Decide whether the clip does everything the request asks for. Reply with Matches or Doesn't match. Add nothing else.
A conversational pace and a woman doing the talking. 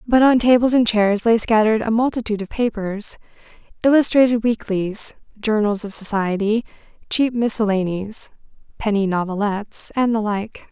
Doesn't match